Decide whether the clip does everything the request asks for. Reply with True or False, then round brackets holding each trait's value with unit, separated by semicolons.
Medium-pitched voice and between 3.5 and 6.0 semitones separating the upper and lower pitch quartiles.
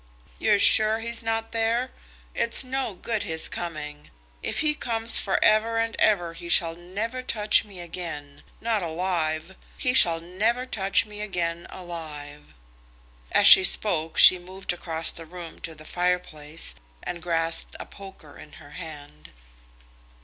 True (180 Hz; 5.1 semitones)